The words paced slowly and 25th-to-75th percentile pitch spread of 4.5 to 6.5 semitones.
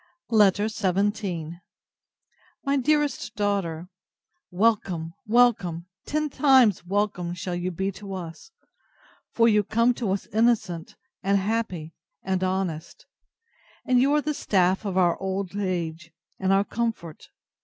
No: slow, 130 wpm; average, 4.1 semitones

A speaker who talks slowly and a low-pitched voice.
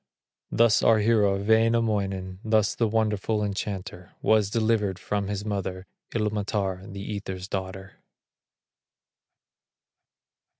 Yes: slow, 95 wpm; low, 105 Hz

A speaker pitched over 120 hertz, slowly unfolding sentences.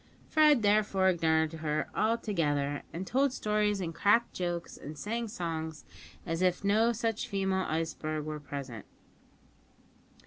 Yes: medium, 185 Hz; slow, 130 wpm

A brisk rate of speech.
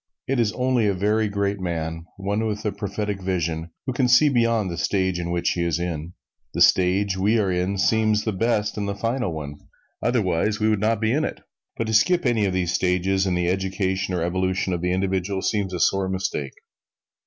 Yes: fast, 210 wpm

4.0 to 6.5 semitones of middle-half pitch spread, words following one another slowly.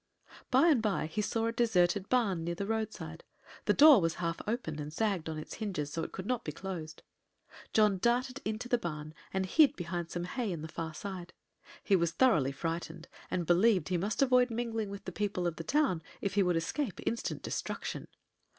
No: average, 5.3 semitones; fast, 205 wpm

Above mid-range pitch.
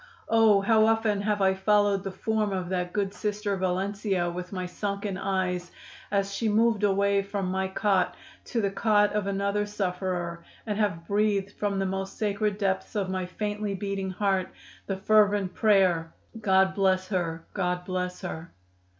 Yes: high, 195 Hz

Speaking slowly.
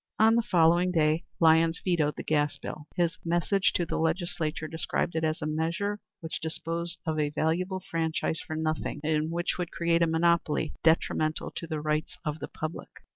No: average, 180 wpm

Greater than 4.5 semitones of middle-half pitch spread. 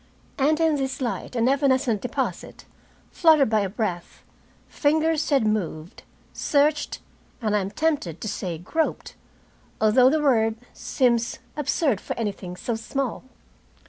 Yes: average, 5.3 semitones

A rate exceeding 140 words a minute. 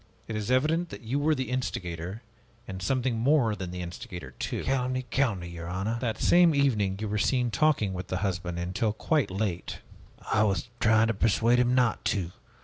Yes: average, 190 wpm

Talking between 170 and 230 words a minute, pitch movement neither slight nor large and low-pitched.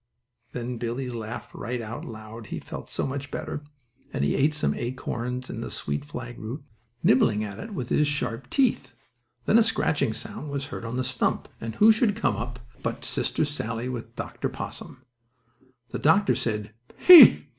Yes: average, 180 wpm; average, 4.1 semitones; low, 125 Hz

